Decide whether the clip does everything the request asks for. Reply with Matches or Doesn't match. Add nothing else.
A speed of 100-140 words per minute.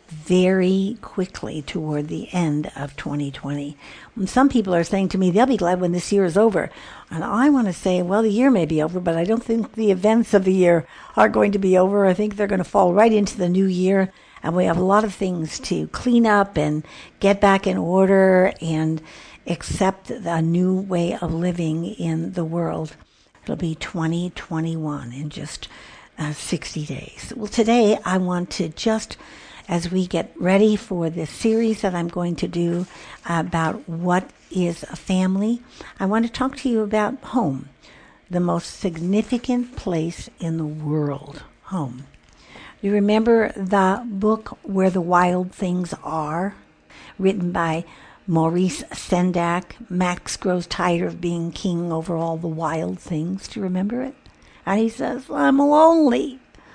Doesn't match